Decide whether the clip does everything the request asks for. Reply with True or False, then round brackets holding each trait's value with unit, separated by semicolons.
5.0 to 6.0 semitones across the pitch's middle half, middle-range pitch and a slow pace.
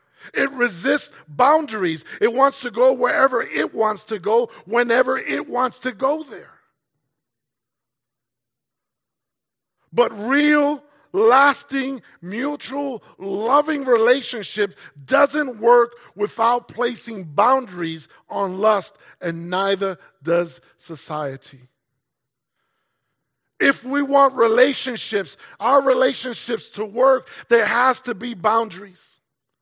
False (5.5 semitones; 235 Hz; 95 wpm)